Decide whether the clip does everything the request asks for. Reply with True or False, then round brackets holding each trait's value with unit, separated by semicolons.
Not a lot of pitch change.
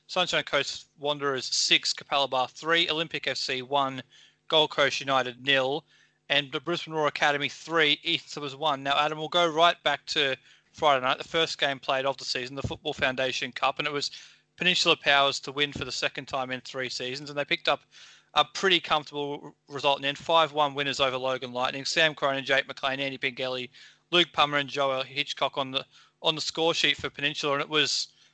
True (2.3 semitones)